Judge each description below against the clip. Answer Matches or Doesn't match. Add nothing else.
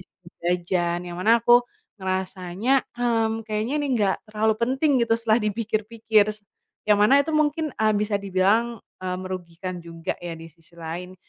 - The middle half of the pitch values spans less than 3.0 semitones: Doesn't match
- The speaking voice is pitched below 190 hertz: Doesn't match